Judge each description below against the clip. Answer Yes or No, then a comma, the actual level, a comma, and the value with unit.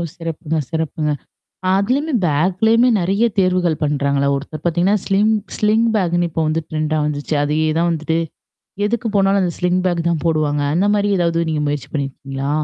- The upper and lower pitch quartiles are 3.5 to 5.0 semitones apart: Yes, average, 4.3 semitones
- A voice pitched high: No, medium, 165 Hz